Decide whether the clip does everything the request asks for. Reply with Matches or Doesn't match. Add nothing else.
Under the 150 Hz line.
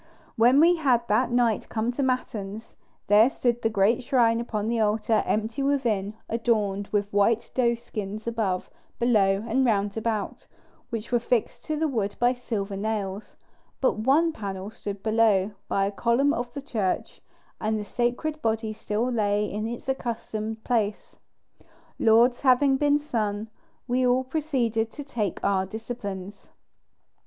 Doesn't match